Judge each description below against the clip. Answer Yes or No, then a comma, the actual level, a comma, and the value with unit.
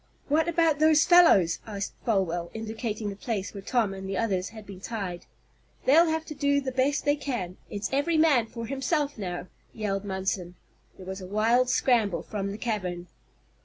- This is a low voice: No, high, 220 Hz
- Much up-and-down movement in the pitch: Yes, wide, 6.5 semitones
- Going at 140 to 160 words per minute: No, average, 180 wpm